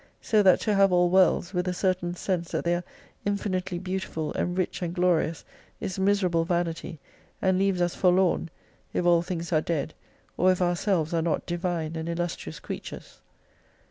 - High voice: No, medium, 175 Hz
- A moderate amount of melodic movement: No, narrow, 1.7 semitones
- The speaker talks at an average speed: Yes, average, 170 wpm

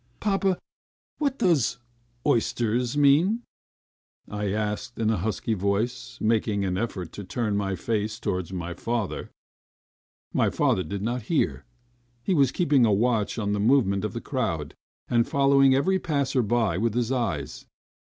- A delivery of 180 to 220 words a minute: No, average, 150 wpm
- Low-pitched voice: Yes, low, 115 Hz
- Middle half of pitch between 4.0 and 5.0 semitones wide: Yes, average, 4.7 semitones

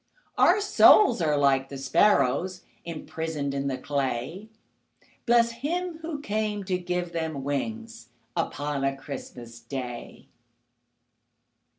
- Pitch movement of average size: No, wide, 8.0 semitones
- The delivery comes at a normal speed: No, slow, 110 wpm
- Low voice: No, medium, 160 Hz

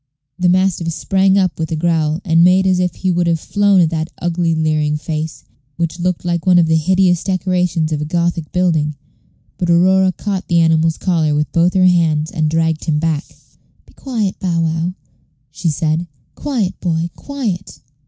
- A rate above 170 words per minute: Yes, average, 185 wpm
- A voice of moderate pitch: Yes, medium, 170 Hz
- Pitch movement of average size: No, narrow, 2.3 semitones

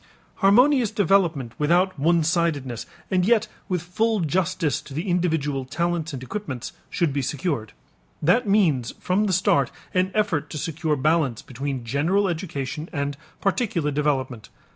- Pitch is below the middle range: No, medium, 165 Hz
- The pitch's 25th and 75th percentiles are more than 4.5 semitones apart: Yes, average, 4.9 semitones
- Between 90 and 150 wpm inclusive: Yes, average, 140 wpm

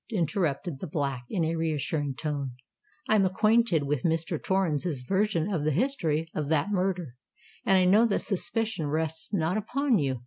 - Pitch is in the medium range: Yes, medium, 165 Hz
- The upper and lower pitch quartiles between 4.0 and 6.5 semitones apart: Yes, average, 4.8 semitones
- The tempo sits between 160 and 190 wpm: Yes, average, 165 wpm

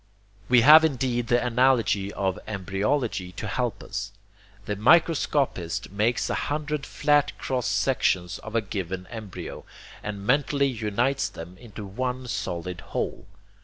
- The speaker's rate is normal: No, slow, 130 wpm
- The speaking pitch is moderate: No, low, 115 Hz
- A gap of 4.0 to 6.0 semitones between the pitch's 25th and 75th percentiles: Yes, average, 5.1 semitones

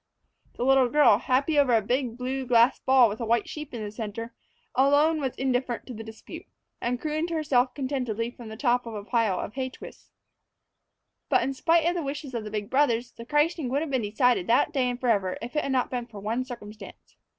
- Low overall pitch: No, very high, 250 Hz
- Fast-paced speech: Yes, fast, 225 wpm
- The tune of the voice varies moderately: Yes, average, 3.1 semitones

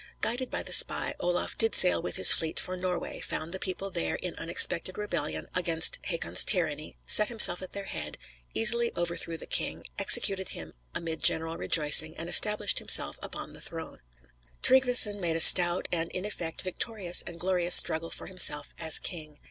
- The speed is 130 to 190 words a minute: Yes, average, 175 wpm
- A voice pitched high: No, medium, 175 Hz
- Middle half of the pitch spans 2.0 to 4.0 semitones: Yes, average, 3.2 semitones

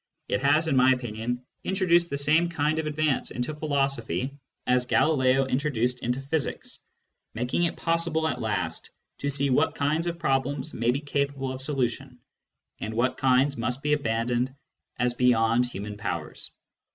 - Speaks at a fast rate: No, average, 155 wpm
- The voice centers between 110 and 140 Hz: Yes, low, 135 Hz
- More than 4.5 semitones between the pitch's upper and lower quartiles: No, average, 3.5 semitones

